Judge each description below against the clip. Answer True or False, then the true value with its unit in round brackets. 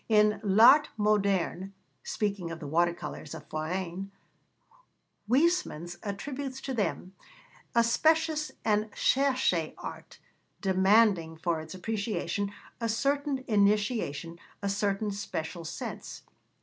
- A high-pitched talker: True (200 Hz)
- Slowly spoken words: True (110 wpm)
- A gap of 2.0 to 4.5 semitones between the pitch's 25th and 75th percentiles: False (5.0 semitones)